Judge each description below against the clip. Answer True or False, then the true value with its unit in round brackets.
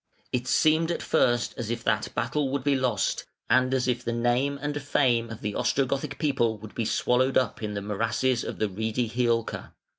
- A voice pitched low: True (125 Hz)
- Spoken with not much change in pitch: False (3.1 semitones)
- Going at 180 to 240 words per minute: True (205 wpm)